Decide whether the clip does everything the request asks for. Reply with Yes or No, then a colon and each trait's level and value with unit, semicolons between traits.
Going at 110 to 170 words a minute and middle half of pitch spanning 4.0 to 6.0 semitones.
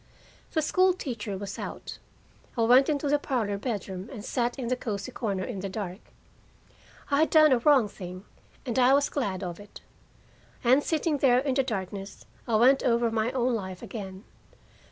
No: average, 180 wpm; average, 5.1 semitones